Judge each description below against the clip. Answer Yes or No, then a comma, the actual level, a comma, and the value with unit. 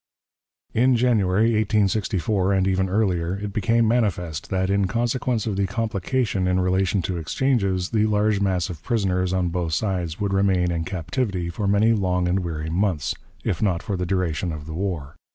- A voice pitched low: Yes, very low, 95 Hz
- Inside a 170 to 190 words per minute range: Yes, average, 175 wpm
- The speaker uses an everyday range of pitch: Yes, average, 3.1 semitones